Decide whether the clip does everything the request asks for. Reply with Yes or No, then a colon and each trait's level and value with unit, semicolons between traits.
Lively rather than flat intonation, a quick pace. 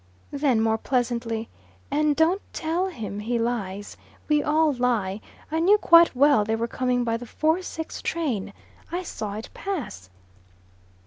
No: wide, 6.2 semitones; average, 150 wpm